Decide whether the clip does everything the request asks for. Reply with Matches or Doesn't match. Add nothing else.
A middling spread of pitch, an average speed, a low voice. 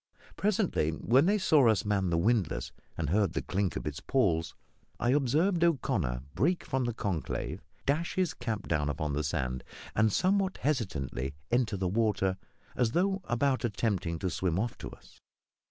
Doesn't match